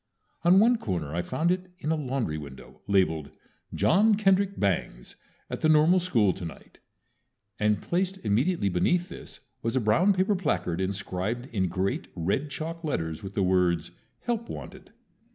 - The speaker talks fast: No, average, 155 wpm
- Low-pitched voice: Yes, low, 120 Hz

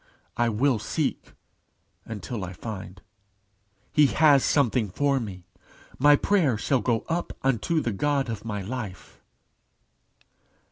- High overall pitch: No, low, 120 Hz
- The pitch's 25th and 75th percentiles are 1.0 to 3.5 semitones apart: No, average, 5.2 semitones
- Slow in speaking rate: Yes, slow, 125 wpm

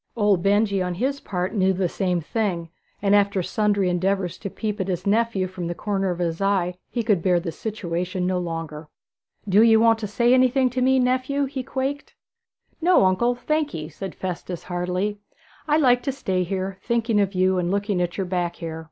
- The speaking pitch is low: No, high, 195 Hz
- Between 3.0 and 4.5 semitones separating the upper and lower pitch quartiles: Yes, average, 4.2 semitones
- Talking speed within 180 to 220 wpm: Yes, average, 200 wpm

